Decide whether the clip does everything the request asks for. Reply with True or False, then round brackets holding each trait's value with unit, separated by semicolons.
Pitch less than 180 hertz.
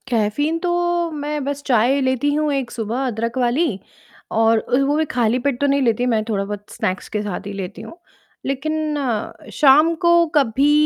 False (260 Hz)